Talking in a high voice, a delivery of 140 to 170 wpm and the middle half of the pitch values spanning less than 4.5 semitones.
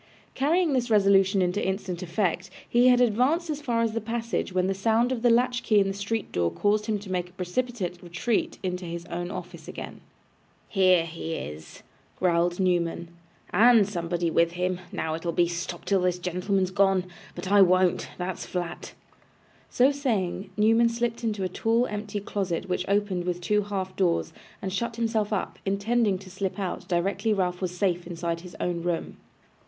No: high, 195 Hz; average, 180 wpm; average, 3.8 semitones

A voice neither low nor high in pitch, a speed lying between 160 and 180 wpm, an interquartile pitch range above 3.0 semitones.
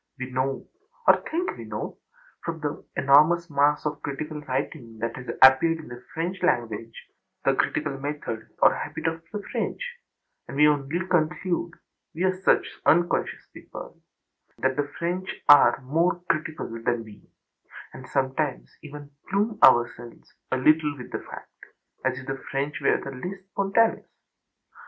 No: medium, 145 Hz; average, 150 wpm; average, 4.3 semitones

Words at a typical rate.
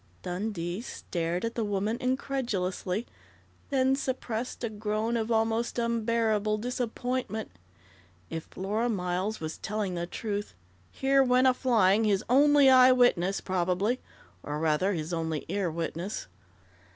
No: slow, 130 wpm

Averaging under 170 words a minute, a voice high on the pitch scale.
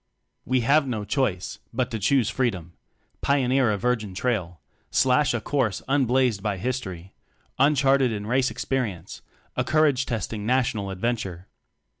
No: average, 145 wpm; low, 120 Hz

